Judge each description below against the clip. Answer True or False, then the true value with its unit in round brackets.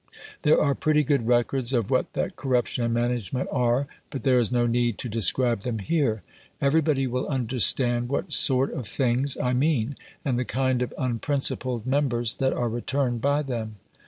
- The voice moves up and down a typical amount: False (2.3 semitones)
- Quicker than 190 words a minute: False (175 wpm)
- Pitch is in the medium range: False (125 Hz)